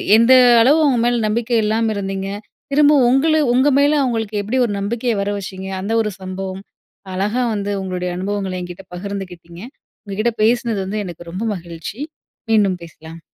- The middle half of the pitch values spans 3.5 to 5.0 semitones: Yes, average, 3.8 semitones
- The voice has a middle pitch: No, high, 205 Hz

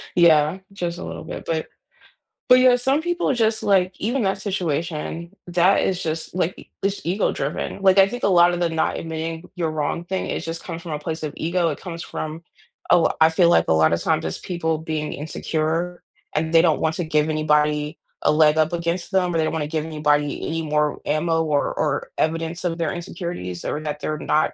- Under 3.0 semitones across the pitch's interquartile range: Yes, narrow, 2.5 semitones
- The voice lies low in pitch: No, medium, 165 Hz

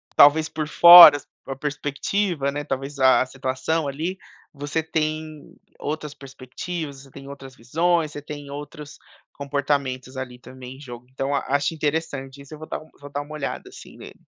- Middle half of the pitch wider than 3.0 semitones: No, narrow, 2.4 semitones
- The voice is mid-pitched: Yes, medium, 145 Hz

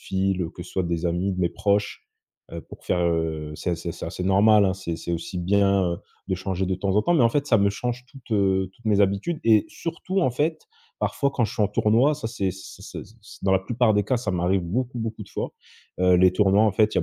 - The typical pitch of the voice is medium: No, low, 100 Hz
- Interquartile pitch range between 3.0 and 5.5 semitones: Yes, average, 3.5 semitones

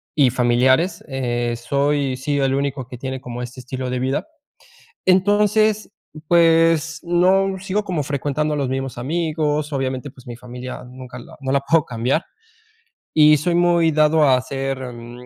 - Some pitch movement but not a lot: Yes, average, 4.3 semitones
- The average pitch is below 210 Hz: Yes, medium, 140 Hz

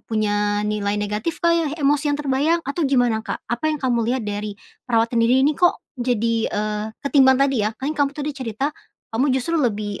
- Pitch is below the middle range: No, high, 245 Hz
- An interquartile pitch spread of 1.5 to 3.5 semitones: No, average, 5.1 semitones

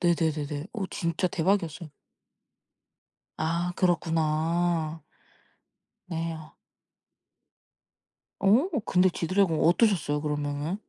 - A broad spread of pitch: No, narrow, 2.6 semitones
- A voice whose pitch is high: No, medium, 165 Hz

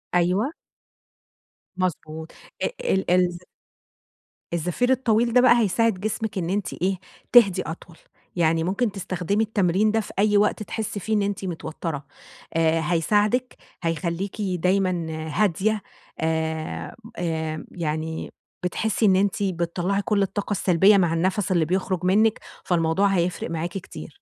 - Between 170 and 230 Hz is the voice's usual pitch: Yes, medium, 185 Hz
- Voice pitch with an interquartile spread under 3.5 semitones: No, average, 3.8 semitones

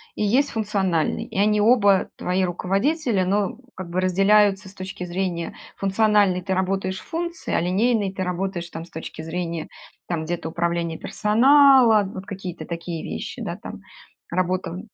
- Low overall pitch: No, high, 190 Hz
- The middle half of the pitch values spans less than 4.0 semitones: Yes, average, 3.1 semitones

